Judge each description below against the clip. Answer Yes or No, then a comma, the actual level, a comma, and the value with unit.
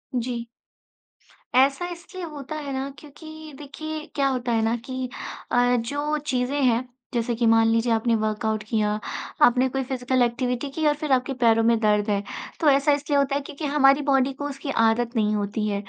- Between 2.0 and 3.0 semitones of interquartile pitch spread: No, average, 3.7 semitones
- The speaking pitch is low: No, very high, 255 Hz